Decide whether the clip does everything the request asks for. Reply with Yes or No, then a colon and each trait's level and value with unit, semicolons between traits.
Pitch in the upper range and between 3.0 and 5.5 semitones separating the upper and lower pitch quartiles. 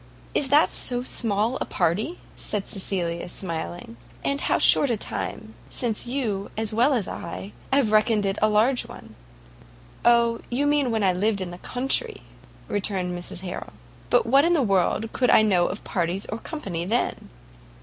Yes: high, 215 Hz; average, 4.9 semitones